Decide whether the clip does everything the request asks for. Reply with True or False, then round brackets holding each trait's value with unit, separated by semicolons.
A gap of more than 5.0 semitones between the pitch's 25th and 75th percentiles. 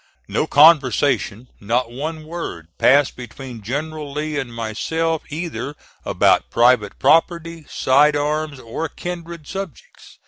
False (4.4 semitones)